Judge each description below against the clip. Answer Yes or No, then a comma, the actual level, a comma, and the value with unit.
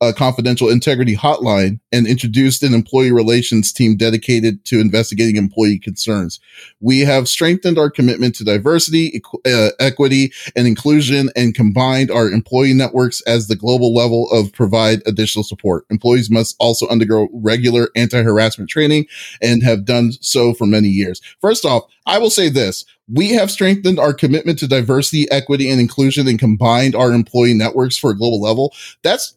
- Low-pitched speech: Yes, low, 120 Hz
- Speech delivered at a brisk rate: No, average, 165 wpm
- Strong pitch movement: No, average, 3.1 semitones